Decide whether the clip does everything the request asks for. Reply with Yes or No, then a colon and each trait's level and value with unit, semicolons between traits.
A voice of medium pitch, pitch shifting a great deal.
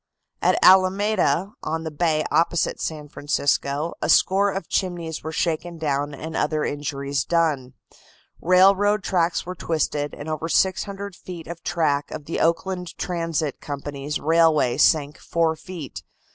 No: medium, 165 Hz; average, 3.4 semitones